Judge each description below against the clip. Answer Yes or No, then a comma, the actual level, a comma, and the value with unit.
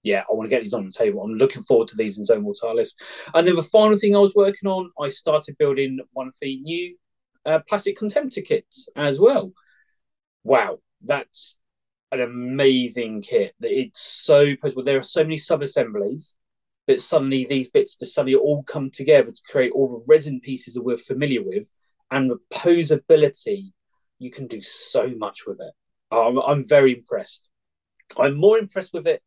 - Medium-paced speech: Yes, average, 185 wpm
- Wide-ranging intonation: Yes, wide, 7.6 semitones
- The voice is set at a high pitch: No, medium, 155 Hz